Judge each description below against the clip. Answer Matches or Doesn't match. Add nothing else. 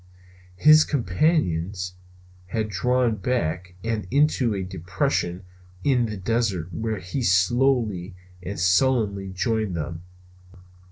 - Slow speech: Matches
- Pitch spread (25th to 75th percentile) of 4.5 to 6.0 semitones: Matches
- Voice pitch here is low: Matches